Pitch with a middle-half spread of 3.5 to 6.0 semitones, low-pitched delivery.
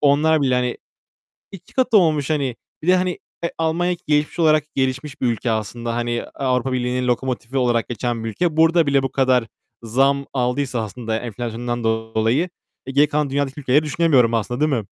Yes: average, 3.9 semitones; low, 130 Hz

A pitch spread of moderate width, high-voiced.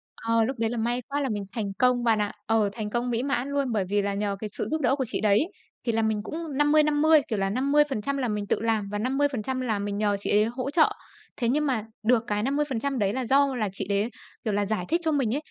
Yes: average, 4.8 semitones; high, 235 Hz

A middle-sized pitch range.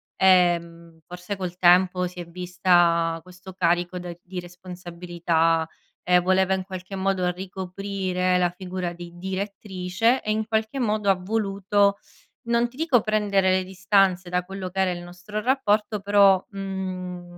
No: narrow, 1.9 semitones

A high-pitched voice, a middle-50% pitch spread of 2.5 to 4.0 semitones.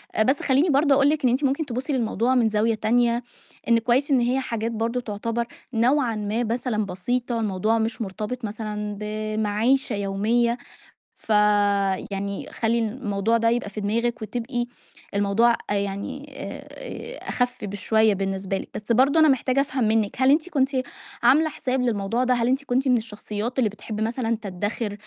Yes: high, 230 Hz; average, 3.3 semitones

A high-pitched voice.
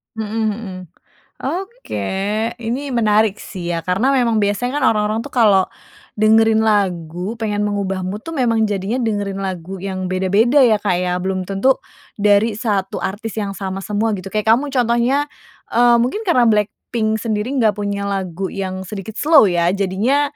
Yes: high, 210 Hz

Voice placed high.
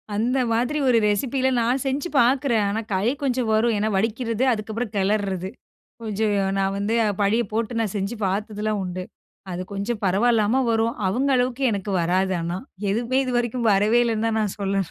Yes: high, 220 Hz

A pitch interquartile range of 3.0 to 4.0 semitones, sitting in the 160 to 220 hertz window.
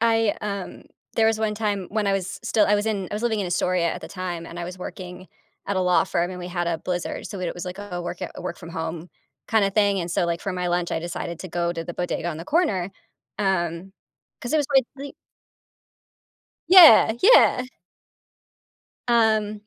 Yes: average, 3.5 semitones; medium, 185 Hz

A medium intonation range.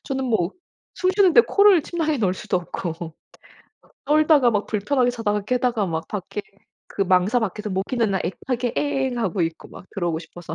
No: wide, 6.2 semitones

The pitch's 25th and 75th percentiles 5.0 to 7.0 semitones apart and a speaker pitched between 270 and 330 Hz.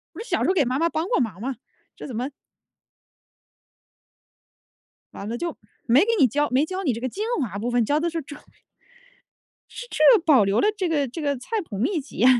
Yes: wide, 5.6 semitones; very high, 280 Hz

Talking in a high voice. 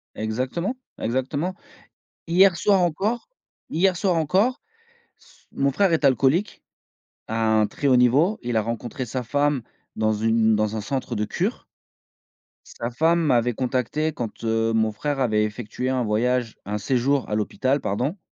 No: low, 130 Hz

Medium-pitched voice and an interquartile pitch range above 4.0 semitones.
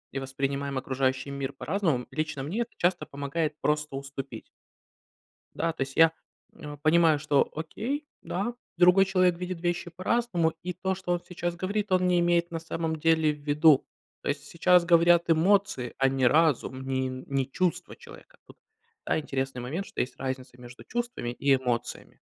Yes: medium, 160 Hz; average, 4.5 semitones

